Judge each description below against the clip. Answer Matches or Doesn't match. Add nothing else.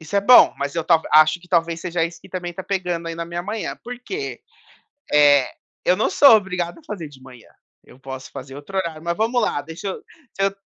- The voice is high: Doesn't match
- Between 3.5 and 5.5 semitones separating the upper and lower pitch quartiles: Matches